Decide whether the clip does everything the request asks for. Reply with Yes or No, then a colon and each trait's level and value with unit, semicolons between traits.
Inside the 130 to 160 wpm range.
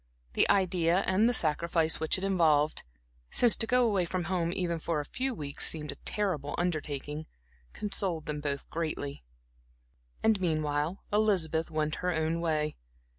Yes: average, 155 wpm